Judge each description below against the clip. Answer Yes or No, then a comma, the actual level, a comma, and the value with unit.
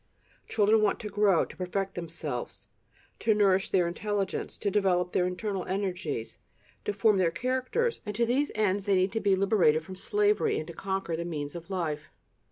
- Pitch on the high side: Yes, high, 195 Hz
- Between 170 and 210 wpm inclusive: Yes, average, 180 wpm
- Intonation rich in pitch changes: No, average, 3.2 semitones